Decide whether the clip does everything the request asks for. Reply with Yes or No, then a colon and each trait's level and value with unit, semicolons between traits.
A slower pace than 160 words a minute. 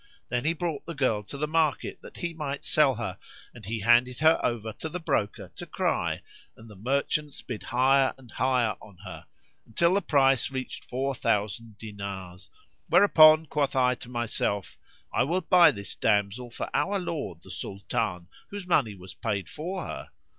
No: average, 175 wpm